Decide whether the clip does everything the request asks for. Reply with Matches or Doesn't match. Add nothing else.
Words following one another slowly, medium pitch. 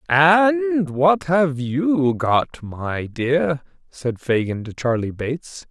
Matches